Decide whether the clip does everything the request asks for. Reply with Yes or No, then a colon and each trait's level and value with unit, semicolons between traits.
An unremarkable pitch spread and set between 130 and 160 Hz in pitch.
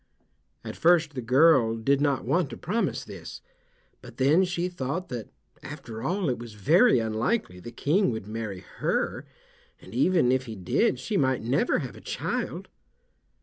No: wide, 7.1 semitones; low, 135 Hz